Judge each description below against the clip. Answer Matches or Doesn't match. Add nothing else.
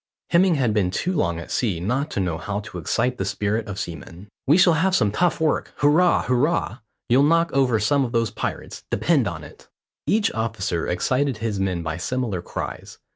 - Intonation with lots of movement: Matches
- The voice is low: Matches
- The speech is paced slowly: Doesn't match